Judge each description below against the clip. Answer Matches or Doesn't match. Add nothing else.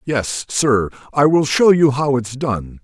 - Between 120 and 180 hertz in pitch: Matches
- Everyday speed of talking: Matches